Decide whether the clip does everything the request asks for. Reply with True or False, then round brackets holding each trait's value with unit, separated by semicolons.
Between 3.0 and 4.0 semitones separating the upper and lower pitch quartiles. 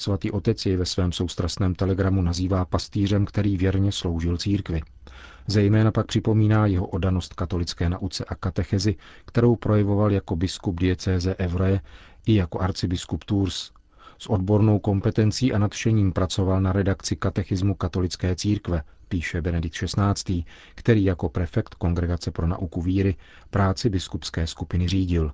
False (2.4 semitones)